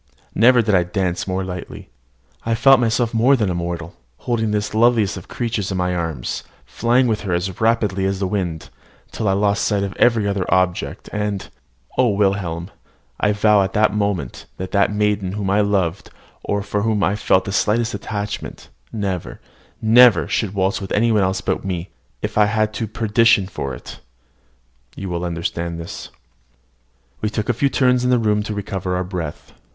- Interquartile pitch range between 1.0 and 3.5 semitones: Yes, average, 2.9 semitones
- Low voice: Yes, low, 100 Hz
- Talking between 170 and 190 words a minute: Yes, average, 185 wpm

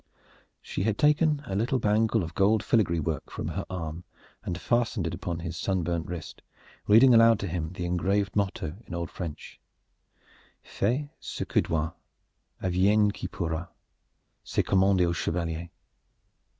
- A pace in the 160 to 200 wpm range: No, average, 150 wpm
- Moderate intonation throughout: Yes, average, 4.0 semitones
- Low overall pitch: Yes, very low, 95 Hz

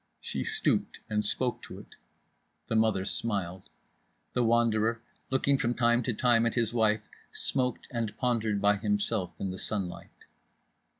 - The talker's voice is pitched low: Yes, low, 110 Hz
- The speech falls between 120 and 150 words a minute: Yes, average, 145 wpm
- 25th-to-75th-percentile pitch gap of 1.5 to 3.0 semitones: Yes, narrow, 2.5 semitones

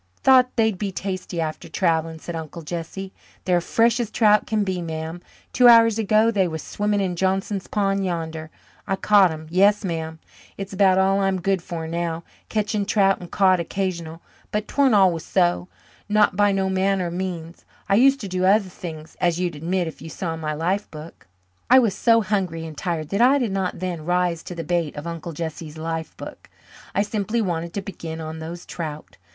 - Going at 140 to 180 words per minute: No, average, 195 wpm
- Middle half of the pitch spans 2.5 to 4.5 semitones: Yes, average, 3.5 semitones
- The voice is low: No, medium, 185 Hz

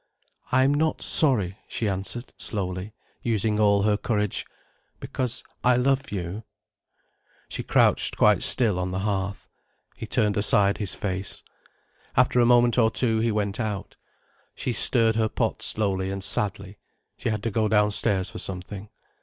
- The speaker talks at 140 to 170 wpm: Yes, average, 150 wpm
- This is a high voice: No, low, 105 Hz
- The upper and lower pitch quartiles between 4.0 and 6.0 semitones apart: No, average, 2.9 semitones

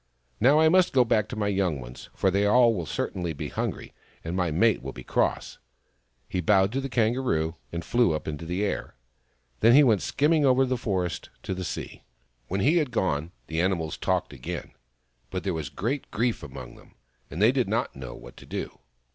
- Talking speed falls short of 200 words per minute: No, fast, 205 wpm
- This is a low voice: Yes, low, 100 Hz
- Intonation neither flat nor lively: No, wide, 7.0 semitones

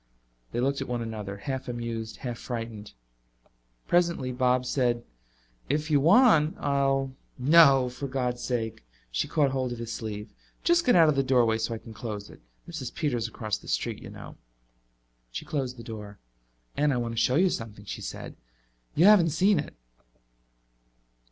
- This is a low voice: Yes, low, 125 Hz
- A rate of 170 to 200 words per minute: Yes, average, 175 wpm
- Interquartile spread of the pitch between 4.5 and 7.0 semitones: No, average, 4.1 semitones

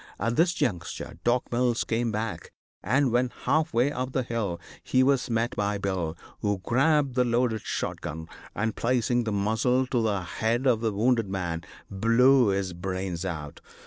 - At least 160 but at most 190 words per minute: Yes, average, 175 wpm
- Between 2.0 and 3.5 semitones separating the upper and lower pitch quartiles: No, average, 4.3 semitones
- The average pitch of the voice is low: Yes, low, 115 Hz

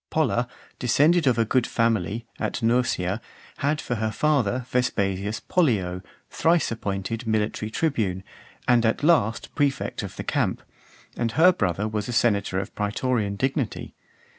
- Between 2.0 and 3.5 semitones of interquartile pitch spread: No, average, 4.0 semitones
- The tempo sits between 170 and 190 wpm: No, average, 145 wpm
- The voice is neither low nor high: No, low, 115 Hz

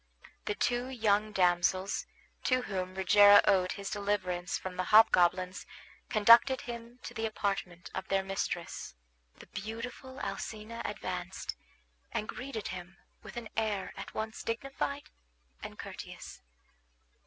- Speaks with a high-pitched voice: Yes, high, 205 Hz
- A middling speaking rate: No, slow, 125 wpm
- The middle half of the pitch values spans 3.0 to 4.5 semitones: Yes, average, 3.4 semitones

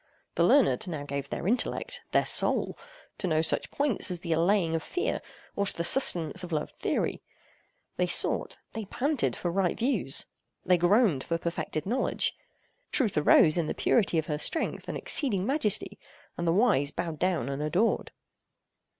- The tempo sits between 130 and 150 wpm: No, average, 160 wpm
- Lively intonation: Yes, wide, 5.9 semitones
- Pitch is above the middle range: No, medium, 180 Hz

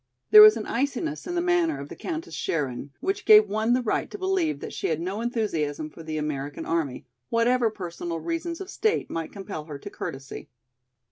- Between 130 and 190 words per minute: No, average, 200 wpm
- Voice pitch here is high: Yes, high, 215 Hz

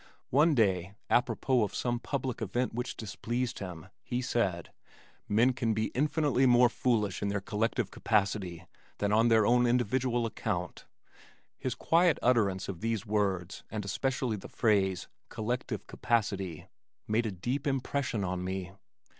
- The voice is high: No, low, 115 Hz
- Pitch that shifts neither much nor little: Yes, average, 4.0 semitones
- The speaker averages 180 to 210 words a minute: No, average, 145 wpm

